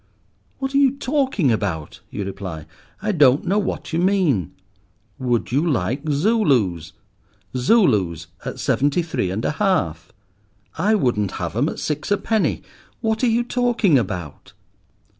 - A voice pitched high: No, medium, 145 Hz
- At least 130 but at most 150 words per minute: Yes, average, 140 wpm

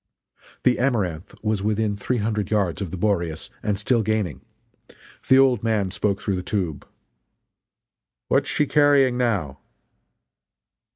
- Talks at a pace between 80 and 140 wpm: Yes, slow, 135 wpm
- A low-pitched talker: Yes, low, 105 Hz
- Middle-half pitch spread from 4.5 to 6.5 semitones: No, average, 3.8 semitones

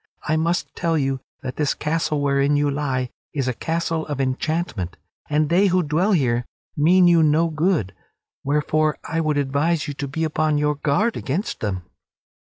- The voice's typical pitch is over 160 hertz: No, medium, 150 Hz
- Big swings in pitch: No, average, 2.9 semitones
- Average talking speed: Yes, average, 175 wpm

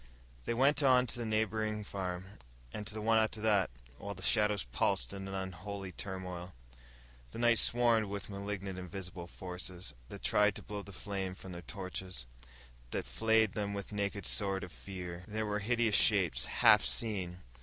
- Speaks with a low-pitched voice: Yes, low, 100 Hz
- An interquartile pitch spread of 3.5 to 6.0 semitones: No, average, 2.8 semitones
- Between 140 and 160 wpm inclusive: No, average, 175 wpm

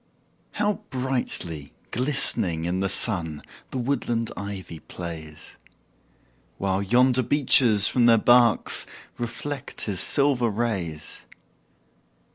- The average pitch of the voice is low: Yes, low, 115 Hz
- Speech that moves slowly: Yes, slow, 95 wpm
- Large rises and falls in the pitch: Yes, wide, 5.9 semitones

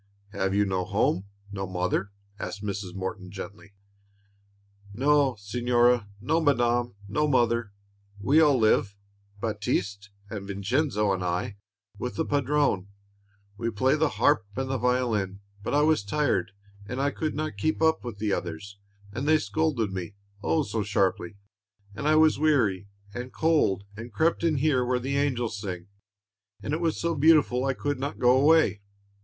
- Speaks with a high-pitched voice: No, low, 120 Hz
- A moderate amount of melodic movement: No, wide, 6.2 semitones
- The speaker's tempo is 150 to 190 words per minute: Yes, average, 160 wpm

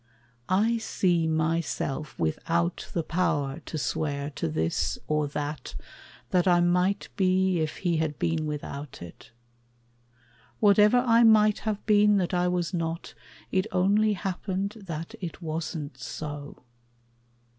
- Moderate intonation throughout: Yes, average, 4.2 semitones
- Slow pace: Yes, slow, 130 wpm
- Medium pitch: Yes, medium, 170 Hz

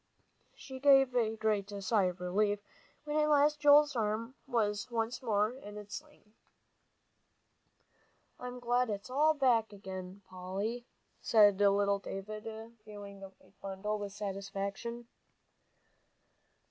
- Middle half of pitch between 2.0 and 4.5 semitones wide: Yes, average, 3.7 semitones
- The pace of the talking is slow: Yes, slow, 120 wpm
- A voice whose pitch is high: Yes, high, 215 Hz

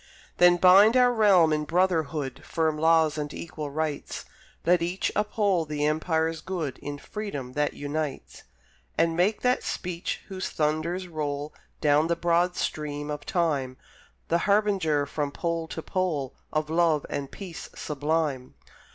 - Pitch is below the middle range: No, medium, 160 Hz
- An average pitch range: Yes, average, 3.2 semitones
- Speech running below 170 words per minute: Yes, average, 140 wpm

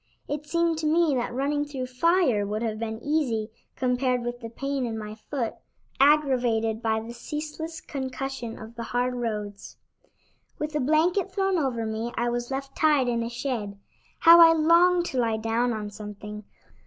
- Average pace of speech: Yes, average, 175 wpm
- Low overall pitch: No, very high, 250 Hz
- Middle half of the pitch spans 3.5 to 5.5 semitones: Yes, average, 5.0 semitones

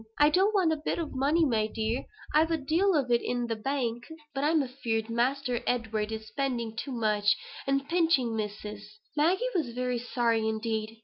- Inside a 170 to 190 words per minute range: Yes, average, 175 wpm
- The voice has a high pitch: Yes, high, 245 Hz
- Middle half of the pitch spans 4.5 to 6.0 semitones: Yes, average, 4.9 semitones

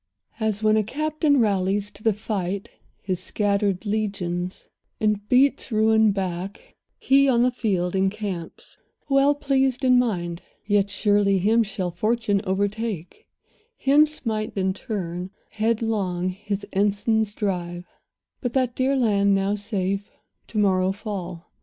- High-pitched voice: Yes, high, 205 Hz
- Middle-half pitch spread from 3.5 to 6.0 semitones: No, average, 3.0 semitones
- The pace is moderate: No, slow, 130 wpm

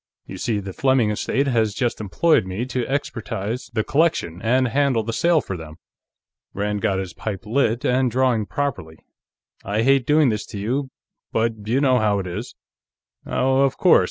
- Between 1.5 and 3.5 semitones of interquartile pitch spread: No, average, 4.4 semitones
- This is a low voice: Yes, low, 115 Hz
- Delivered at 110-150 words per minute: No, average, 180 wpm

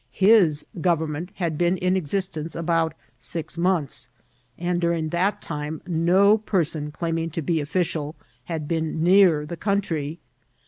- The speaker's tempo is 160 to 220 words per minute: No, slow, 135 wpm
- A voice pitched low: No, medium, 165 Hz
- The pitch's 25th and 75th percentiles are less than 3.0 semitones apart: Yes, narrow, 2.6 semitones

